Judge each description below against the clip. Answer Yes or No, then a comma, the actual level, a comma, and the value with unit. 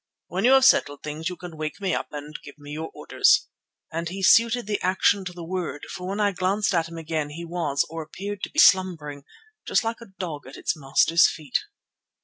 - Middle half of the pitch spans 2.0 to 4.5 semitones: Yes, average, 4.2 semitones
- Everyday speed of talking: No, fast, 220 wpm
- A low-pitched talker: No, medium, 170 Hz